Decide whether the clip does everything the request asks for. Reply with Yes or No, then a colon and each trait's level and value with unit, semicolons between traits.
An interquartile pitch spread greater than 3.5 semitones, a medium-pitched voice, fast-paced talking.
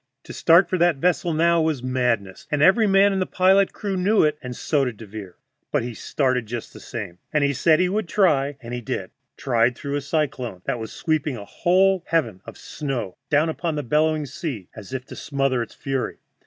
Yes: wide, 5.6 semitones; medium, 145 Hz; fast, 210 wpm